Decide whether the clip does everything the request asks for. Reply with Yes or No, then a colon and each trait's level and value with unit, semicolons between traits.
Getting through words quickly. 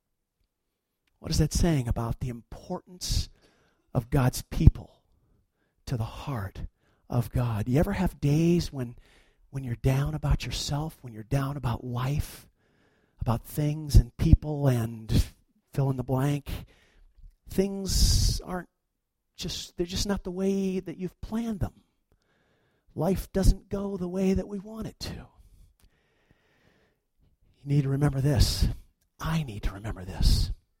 No: average, 140 wpm